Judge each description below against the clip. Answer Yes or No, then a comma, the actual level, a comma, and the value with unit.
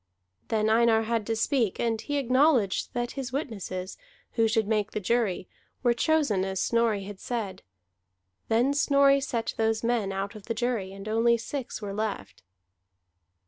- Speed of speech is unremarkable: Yes, average, 160 wpm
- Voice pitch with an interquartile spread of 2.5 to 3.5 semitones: Yes, average, 2.9 semitones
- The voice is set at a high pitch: Yes, high, 225 Hz